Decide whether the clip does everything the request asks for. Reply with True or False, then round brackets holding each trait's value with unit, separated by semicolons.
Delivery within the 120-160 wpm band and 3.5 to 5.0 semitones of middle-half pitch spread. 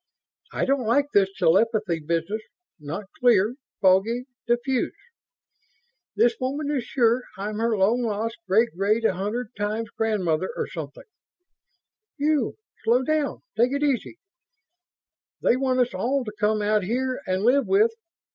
True (140 wpm; 3.8 semitones)